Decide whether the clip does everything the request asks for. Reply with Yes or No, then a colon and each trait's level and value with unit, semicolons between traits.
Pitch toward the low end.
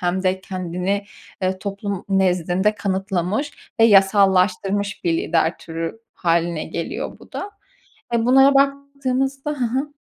No: high, 195 Hz